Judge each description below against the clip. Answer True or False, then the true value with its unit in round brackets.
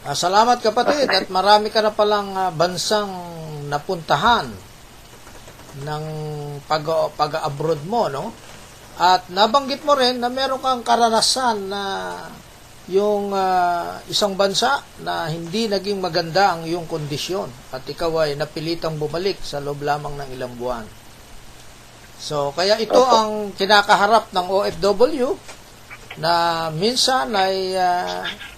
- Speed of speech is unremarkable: True (120 wpm)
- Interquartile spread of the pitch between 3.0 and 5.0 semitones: False (5.6 semitones)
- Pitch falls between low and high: True (180 Hz)